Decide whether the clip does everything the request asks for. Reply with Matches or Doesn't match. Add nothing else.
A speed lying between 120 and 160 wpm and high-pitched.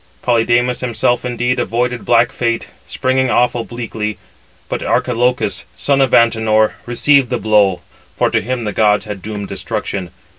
Doesn't match